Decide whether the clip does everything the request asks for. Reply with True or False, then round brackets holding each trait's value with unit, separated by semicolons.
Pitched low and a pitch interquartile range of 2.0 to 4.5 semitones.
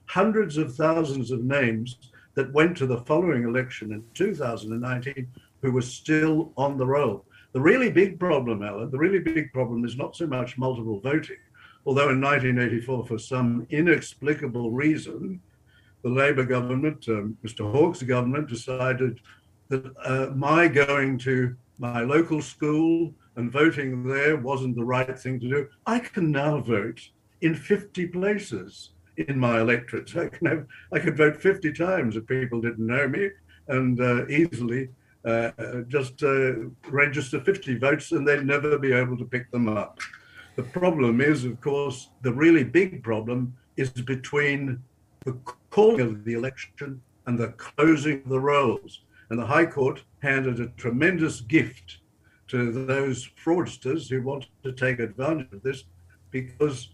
True (130 Hz; 3.8 semitones)